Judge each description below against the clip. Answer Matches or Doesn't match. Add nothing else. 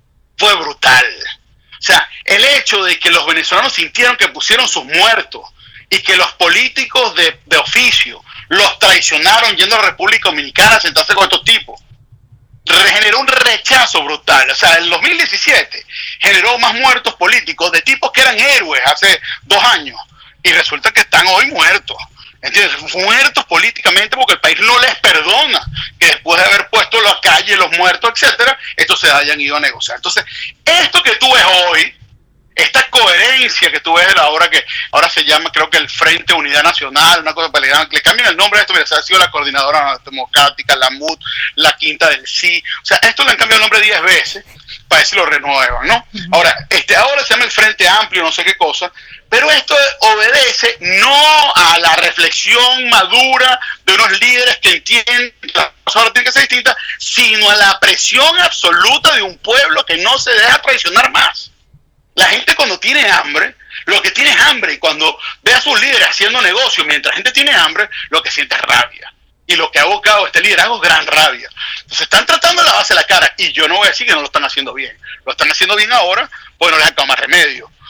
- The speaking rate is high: Matches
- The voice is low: Doesn't match